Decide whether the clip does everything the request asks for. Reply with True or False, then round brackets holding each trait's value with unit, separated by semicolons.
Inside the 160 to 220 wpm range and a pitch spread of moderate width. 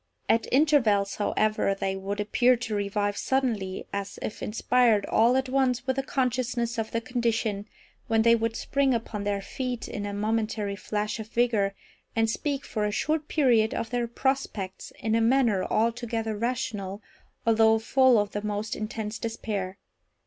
True (165 wpm; 3.0 semitones)